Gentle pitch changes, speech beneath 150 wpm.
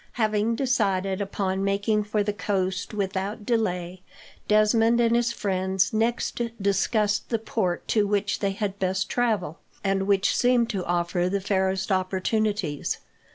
Yes: narrow, 2.3 semitones; average, 140 wpm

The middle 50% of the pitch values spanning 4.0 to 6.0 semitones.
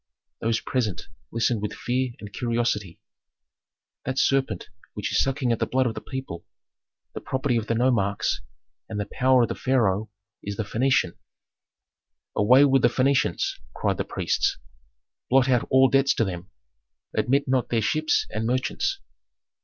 No: average, 3.4 semitones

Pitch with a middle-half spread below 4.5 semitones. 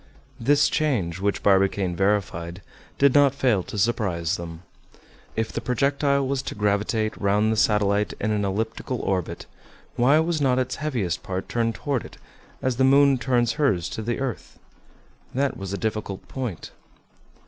No: average, 5.1 semitones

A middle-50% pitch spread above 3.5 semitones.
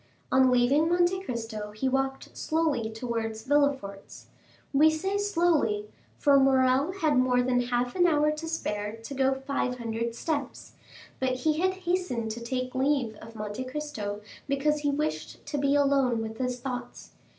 Yes: average, 4.3 semitones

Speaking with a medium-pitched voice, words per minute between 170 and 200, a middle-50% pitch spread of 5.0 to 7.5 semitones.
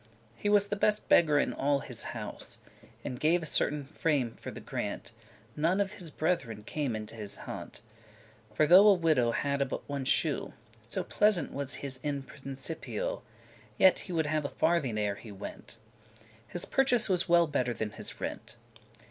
Yes: medium, 150 Hz; average, 180 wpm; wide, 5.5 semitones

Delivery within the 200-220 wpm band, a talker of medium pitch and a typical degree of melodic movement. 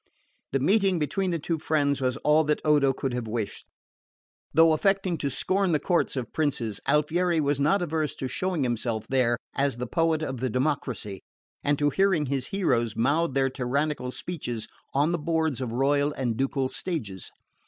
No: average, 175 wpm; medium, 145 Hz; average, 4.1 semitones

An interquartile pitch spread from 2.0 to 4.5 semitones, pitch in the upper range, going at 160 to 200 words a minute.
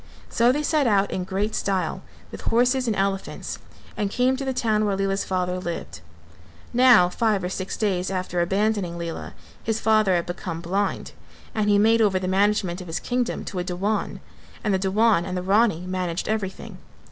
Yes: average, 3.1 semitones; high, 195 Hz; average, 185 wpm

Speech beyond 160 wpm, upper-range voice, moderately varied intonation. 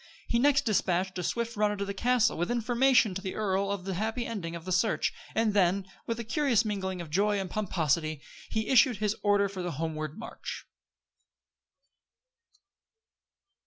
Yes: average, 170 wpm; high, 200 Hz; average, 3.6 semitones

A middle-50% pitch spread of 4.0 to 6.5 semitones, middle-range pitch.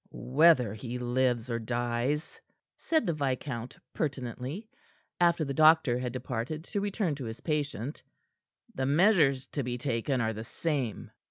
No: average, 4.3 semitones; low, 130 Hz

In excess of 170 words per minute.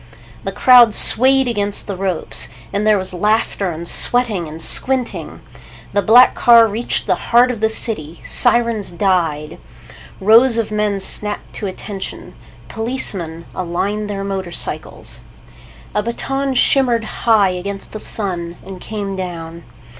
No: slow, 135 wpm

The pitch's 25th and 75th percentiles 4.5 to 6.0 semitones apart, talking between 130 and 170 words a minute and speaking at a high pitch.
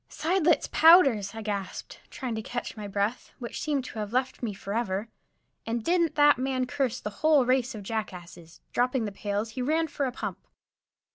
No: average, 4.9 semitones; average, 185 wpm; high, 245 Hz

